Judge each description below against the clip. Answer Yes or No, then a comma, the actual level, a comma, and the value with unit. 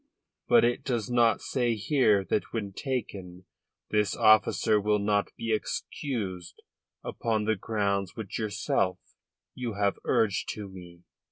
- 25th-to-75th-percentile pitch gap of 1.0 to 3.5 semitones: Yes, narrow, 2.6 semitones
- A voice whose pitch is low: Yes, low, 105 Hz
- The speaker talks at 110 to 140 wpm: Yes, slow, 135 wpm